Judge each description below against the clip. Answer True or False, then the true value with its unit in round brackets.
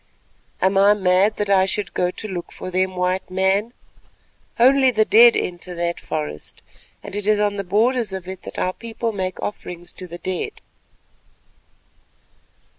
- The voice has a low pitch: False (190 Hz)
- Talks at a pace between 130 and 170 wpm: True (165 wpm)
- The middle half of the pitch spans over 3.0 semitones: False (2.6 semitones)